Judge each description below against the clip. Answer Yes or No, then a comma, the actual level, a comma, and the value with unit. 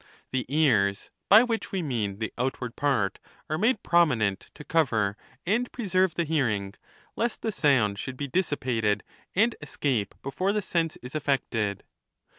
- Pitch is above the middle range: No, medium, 140 Hz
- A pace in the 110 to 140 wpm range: No, average, 150 wpm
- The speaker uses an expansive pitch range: Yes, wide, 7.9 semitones